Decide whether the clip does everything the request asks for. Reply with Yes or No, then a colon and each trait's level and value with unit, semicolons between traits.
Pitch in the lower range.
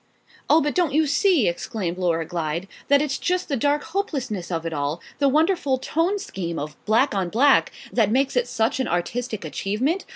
No: high, 245 Hz